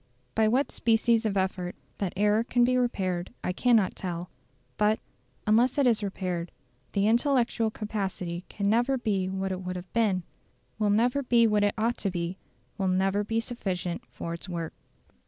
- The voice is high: Yes, high, 205 Hz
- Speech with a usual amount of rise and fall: Yes, average, 3.8 semitones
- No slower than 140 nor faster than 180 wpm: Yes, average, 175 wpm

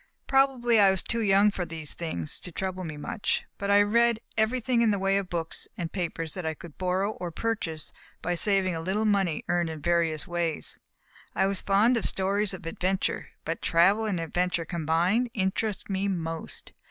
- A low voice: No, high, 190 Hz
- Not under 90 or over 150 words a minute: No, average, 190 wpm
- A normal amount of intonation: Yes, average, 3.6 semitones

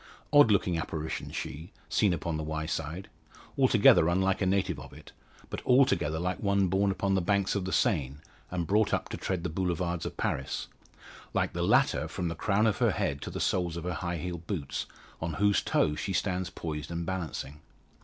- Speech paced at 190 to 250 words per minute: Yes, average, 195 wpm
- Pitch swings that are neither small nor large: Yes, average, 3.4 semitones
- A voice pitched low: Yes, very low, 90 Hz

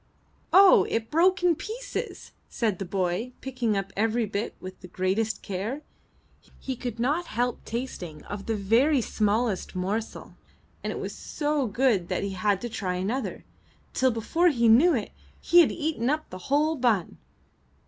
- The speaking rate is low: No, average, 165 wpm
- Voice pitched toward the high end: Yes, high, 230 Hz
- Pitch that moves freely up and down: Yes, wide, 5.7 semitones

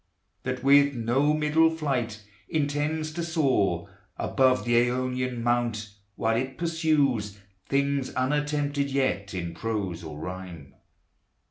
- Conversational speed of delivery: No, slow, 115 wpm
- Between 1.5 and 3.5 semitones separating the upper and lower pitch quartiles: No, average, 4.6 semitones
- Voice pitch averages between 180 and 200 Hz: No, low, 130 Hz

